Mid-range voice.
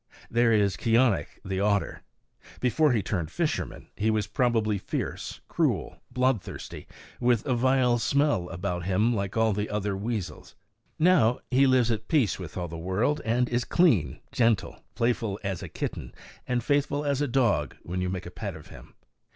No: low, 110 Hz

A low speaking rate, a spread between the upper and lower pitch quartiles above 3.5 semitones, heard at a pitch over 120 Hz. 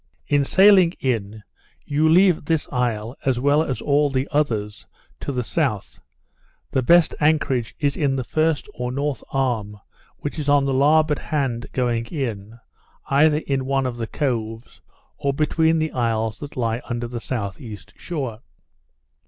No: average, 160 wpm; average, 4.1 semitones; low, 135 Hz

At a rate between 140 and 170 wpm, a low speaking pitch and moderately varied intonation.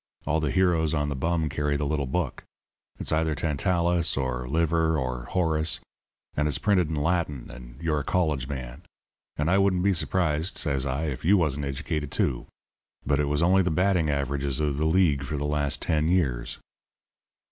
No: average, 185 wpm; very low, 75 Hz; average, 3.2 semitones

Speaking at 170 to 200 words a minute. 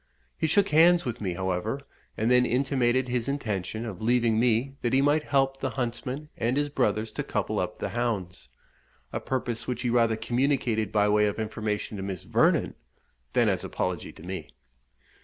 Yes: average, 180 wpm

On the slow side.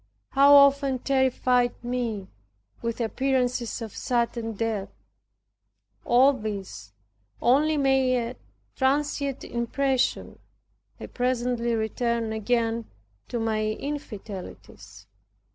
Yes: slow, 90 wpm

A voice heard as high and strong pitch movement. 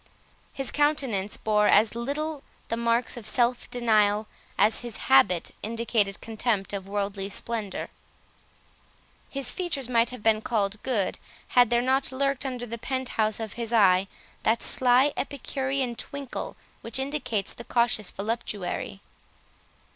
No: high, 235 Hz; average, 3.6 semitones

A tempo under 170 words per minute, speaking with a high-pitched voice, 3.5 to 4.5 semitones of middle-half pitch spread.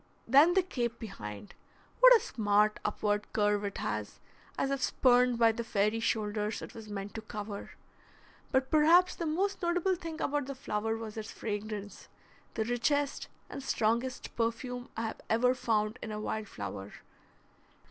Yes: average, 160 wpm; high, 225 Hz; average, 4.2 semitones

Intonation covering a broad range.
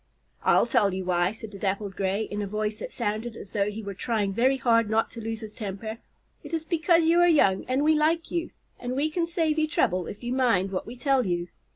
Yes: wide, 6.2 semitones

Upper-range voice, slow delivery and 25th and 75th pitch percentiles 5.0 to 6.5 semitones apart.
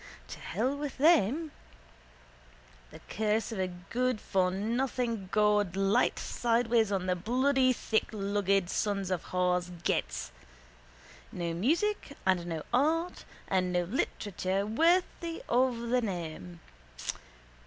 Yes: high, 210 Hz; slow, 110 wpm; wide, 5.5 semitones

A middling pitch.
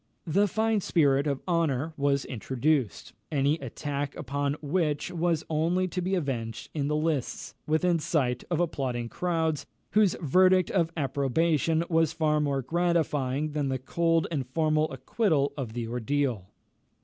Yes: medium, 150 Hz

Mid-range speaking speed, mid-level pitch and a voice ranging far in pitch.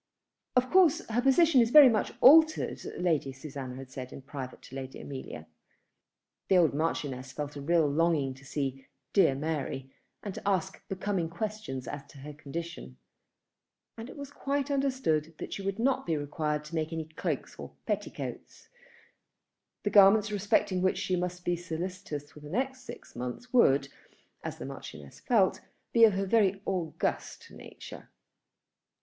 Yes: average, 165 wpm; medium, 170 Hz; wide, 7.0 semitones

